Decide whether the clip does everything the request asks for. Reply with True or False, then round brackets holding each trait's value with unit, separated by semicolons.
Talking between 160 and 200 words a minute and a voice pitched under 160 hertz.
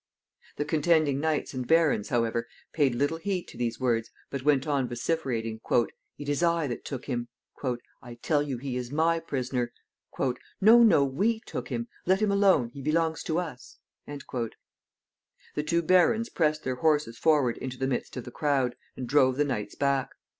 True (175 wpm; 140 Hz)